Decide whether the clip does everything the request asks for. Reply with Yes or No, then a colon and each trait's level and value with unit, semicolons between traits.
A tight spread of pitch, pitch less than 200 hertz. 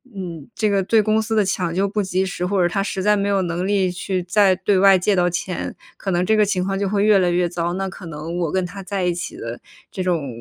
Yes: narrow, 2.2 semitones; high, 190 Hz